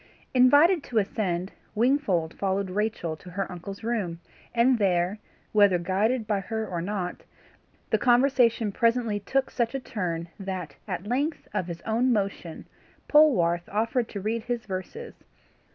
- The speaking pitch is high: Yes, high, 210 Hz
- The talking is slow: No, average, 145 wpm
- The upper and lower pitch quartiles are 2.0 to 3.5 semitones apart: No, average, 4.7 semitones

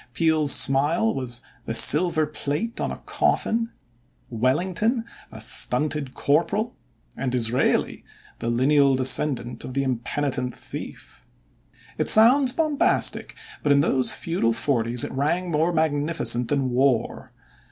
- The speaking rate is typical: No, slow, 120 wpm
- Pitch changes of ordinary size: Yes, average, 4.7 semitones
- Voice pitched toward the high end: No, medium, 145 Hz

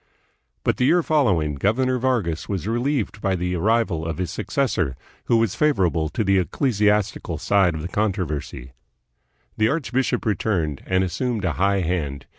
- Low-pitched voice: Yes, low, 100 Hz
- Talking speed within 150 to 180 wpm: Yes, average, 155 wpm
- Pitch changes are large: Yes, wide, 5.7 semitones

